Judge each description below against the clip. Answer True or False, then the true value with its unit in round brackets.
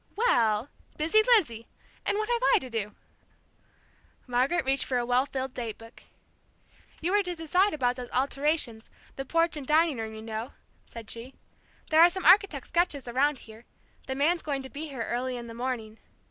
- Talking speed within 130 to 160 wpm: False (185 wpm)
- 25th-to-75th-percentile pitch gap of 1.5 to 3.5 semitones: False (5.5 semitones)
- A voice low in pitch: False (265 Hz)